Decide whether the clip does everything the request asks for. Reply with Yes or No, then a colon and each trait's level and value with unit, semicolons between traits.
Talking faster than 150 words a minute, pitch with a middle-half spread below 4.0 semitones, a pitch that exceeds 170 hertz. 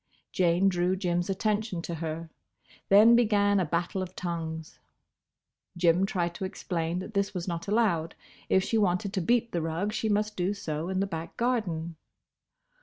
Yes: average, 170 wpm; average, 3.2 semitones; medium, 185 Hz